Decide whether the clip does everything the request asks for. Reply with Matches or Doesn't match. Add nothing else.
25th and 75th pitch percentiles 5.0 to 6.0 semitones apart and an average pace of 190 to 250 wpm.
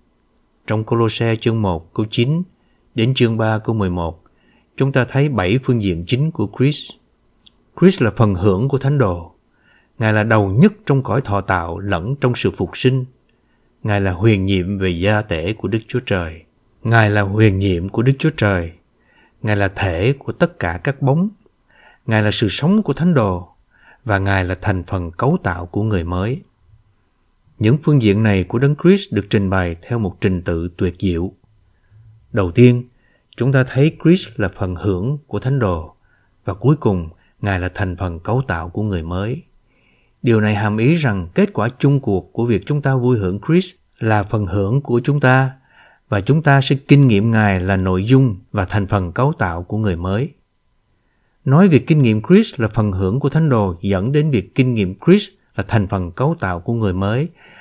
Matches